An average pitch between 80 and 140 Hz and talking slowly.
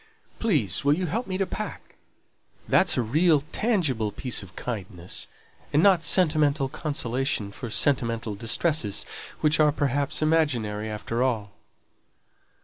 Yes: low, 135 Hz; slow, 130 wpm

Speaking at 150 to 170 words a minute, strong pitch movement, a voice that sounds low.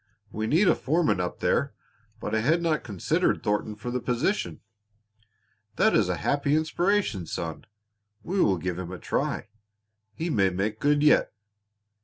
Yes: average, 160 wpm; wide, 8.3 semitones; low, 125 Hz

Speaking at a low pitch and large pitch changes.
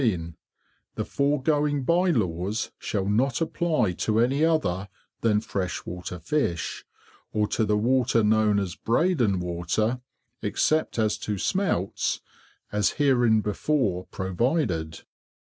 Yes: low, 110 Hz; wide, 6.4 semitones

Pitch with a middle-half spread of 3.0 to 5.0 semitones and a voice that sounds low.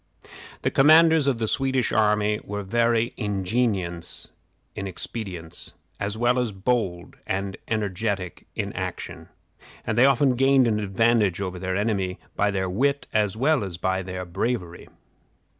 Yes: average, 4.2 semitones; low, 105 Hz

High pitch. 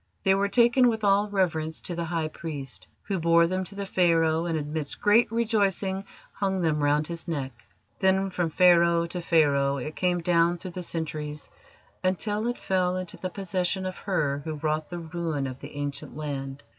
No: medium, 170 Hz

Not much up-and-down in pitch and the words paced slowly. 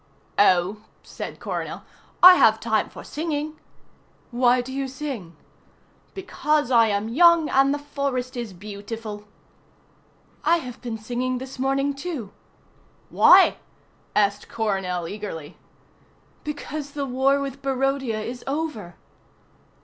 No: average, 4.8 semitones; slow, 120 wpm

